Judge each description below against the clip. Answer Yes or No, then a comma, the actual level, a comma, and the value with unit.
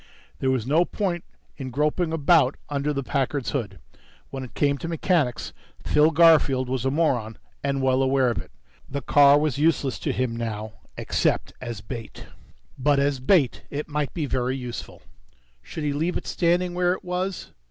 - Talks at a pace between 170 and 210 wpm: Yes, average, 175 wpm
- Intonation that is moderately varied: Yes, average, 3.8 semitones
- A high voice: No, medium, 140 Hz